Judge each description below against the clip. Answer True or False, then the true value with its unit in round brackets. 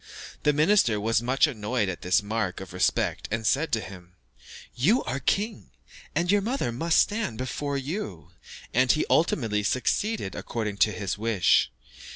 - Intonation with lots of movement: True (6.8 semitones)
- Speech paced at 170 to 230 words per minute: False (160 wpm)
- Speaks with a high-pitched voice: False (120 Hz)